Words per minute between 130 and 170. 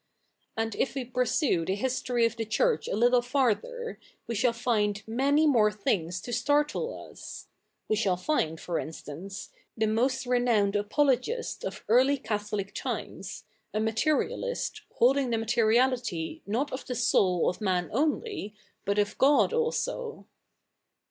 Yes: average, 140 wpm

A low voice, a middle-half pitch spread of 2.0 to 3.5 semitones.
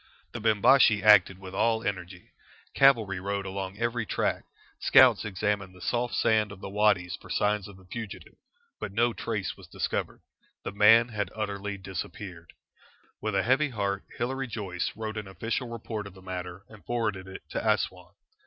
Yes: low, 105 Hz; average, 2.8 semitones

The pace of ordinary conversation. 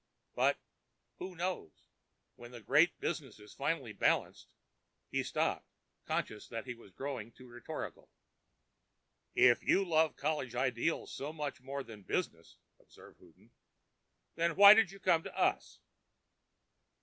No: slow, 125 wpm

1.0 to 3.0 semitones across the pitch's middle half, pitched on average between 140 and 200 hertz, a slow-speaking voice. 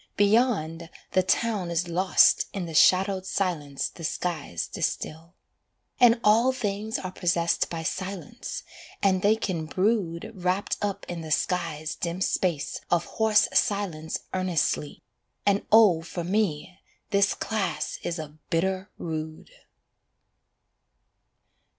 No: average, 3.6 semitones; medium, 185 Hz; slow, 120 wpm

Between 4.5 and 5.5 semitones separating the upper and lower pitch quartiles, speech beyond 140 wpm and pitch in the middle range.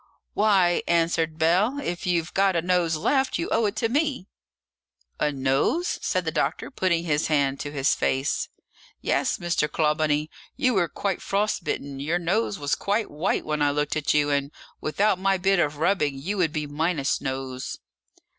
Yes: average, 4.8 semitones; average, 175 wpm; medium, 165 Hz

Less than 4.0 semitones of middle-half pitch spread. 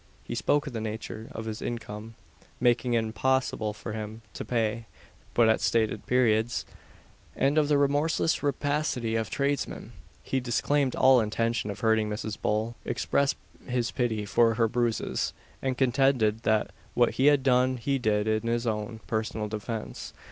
Yes: average, 3.1 semitones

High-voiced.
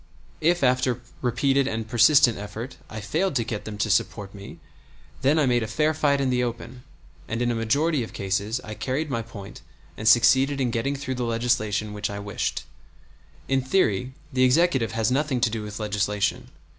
No: low, 120 Hz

